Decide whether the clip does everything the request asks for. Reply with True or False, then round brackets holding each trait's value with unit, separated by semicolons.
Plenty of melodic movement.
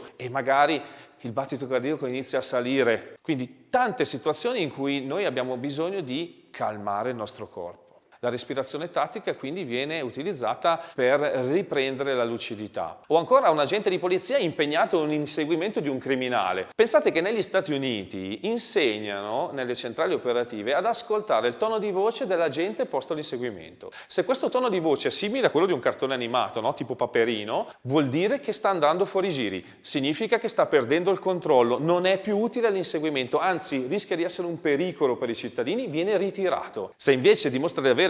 True (7.2 semitones)